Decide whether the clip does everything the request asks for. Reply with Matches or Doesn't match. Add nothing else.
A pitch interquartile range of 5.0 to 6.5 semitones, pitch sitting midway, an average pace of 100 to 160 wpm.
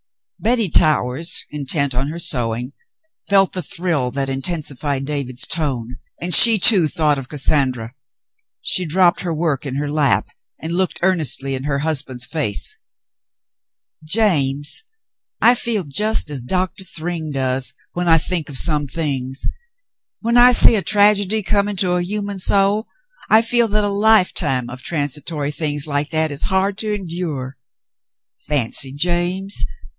Matches